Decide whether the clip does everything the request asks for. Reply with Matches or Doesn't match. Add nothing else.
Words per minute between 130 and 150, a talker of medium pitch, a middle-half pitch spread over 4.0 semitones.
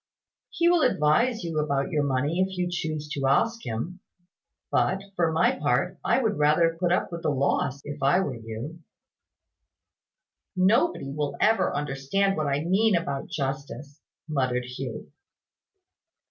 Matches